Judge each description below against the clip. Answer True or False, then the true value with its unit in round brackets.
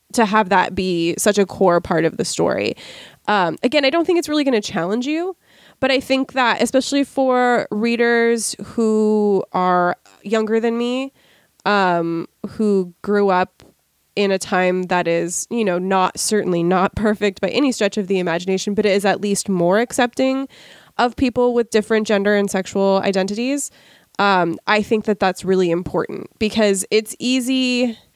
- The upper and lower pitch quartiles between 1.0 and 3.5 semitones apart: False (4.2 semitones)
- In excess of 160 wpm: True (170 wpm)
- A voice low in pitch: False (210 Hz)